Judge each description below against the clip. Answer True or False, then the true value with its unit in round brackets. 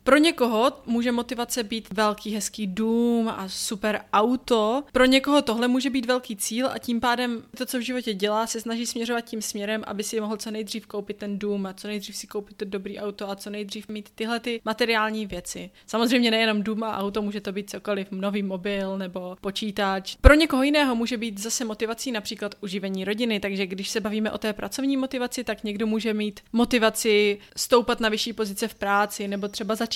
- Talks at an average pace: False (200 wpm)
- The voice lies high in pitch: True (220 Hz)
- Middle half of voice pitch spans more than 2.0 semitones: True (2.4 semitones)